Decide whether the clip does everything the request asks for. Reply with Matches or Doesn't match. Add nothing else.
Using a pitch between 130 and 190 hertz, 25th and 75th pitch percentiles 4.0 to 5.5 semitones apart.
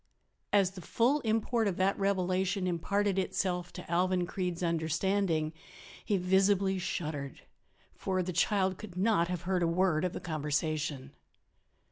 Doesn't match